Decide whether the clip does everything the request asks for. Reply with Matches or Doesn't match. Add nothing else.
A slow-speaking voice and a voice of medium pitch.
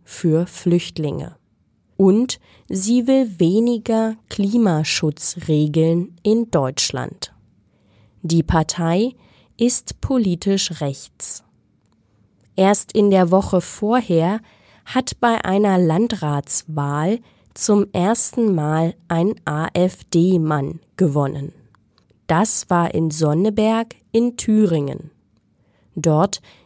Matches